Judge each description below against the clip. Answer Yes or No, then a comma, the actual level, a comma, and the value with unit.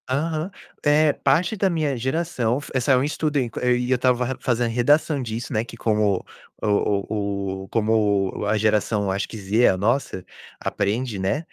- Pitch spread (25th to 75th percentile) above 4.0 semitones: Yes, average, 5.1 semitones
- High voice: No, low, 120 Hz